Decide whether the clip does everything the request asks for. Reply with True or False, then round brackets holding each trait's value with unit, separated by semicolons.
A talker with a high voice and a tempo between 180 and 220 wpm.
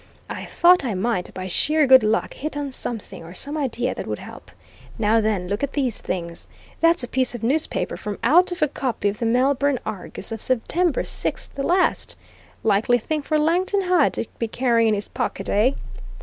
True (250 Hz; 195 wpm)